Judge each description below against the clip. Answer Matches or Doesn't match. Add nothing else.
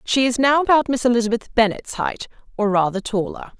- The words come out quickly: Doesn't match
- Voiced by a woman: Matches